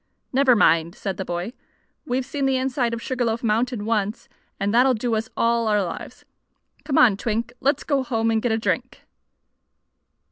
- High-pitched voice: Yes, high, 230 Hz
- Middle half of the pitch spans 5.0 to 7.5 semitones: No, average, 3.1 semitones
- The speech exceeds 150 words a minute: Yes, average, 180 wpm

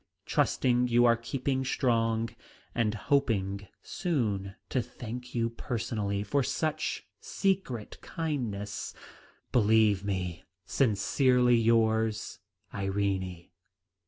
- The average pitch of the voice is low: Yes, low, 115 Hz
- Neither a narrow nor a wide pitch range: Yes, average, 3.5 semitones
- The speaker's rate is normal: No, slow, 90 wpm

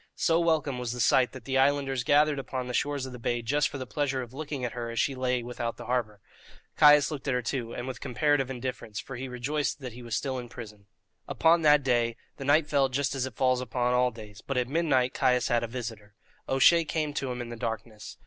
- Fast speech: Yes, fast, 245 wpm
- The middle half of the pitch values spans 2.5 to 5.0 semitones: Yes, average, 2.9 semitones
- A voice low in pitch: Yes, low, 130 Hz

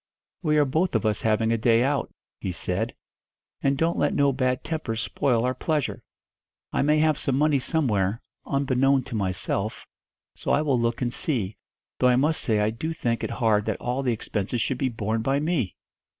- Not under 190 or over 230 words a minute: Yes, average, 195 wpm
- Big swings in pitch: No, average, 4.1 semitones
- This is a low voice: Yes, low, 125 Hz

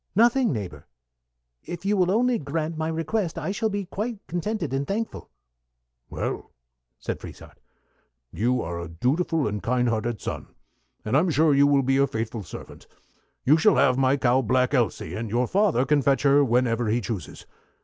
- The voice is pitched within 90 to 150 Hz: Yes, medium, 140 Hz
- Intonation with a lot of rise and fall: Yes, wide, 6.6 semitones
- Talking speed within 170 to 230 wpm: Yes, average, 175 wpm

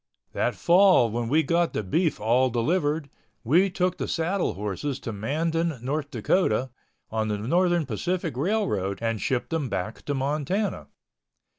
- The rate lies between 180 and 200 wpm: No, average, 150 wpm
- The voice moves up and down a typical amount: No, wide, 7.0 semitones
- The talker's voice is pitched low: No, medium, 145 Hz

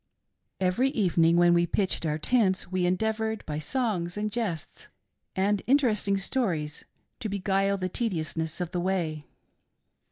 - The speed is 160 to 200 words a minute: No, slow, 135 wpm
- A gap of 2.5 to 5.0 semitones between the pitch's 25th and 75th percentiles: Yes, average, 3.8 semitones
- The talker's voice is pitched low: No, high, 190 Hz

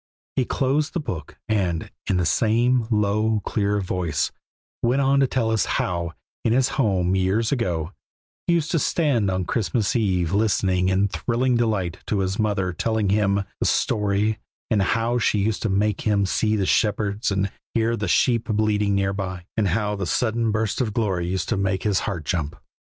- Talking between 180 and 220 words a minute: Yes, average, 185 wpm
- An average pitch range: Yes, average, 3.1 semitones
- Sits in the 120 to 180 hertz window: No, low, 105 Hz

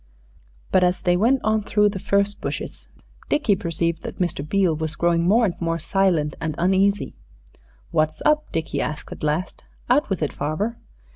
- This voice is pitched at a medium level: Yes, medium, 180 Hz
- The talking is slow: No, average, 170 wpm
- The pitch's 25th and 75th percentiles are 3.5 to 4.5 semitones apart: Yes, average, 4.0 semitones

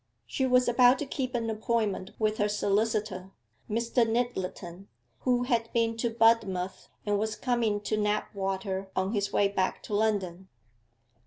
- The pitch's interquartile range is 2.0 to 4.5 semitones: Yes, average, 2.9 semitones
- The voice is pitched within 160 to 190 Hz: No, high, 215 Hz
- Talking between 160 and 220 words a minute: No, average, 150 wpm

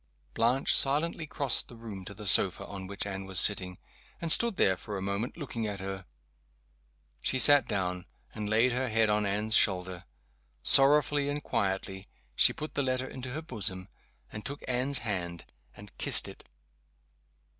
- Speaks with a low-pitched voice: Yes, low, 110 Hz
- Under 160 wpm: No, average, 170 wpm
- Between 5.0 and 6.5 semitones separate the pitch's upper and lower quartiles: Yes, wide, 5.5 semitones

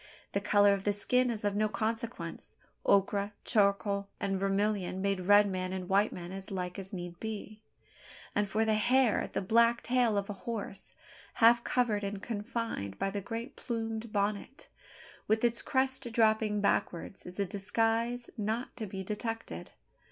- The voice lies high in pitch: Yes, high, 210 Hz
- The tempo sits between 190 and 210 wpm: No, average, 165 wpm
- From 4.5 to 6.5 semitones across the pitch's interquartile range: No, narrow, 2.5 semitones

